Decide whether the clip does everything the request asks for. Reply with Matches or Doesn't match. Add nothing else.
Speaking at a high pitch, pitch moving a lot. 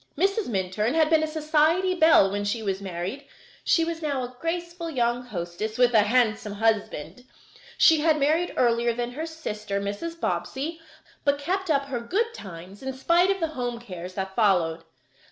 Matches